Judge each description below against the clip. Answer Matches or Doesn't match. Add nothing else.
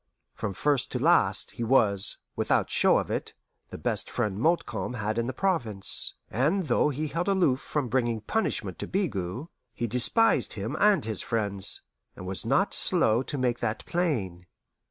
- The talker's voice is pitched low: Matches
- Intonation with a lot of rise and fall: Matches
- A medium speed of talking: Matches